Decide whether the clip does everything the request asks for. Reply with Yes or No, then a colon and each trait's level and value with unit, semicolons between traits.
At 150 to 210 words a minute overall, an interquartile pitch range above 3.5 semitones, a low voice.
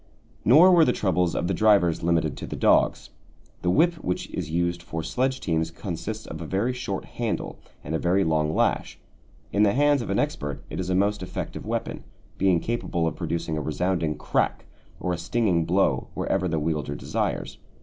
Yes: average, 190 wpm; average, 4.3 semitones; very low, 90 Hz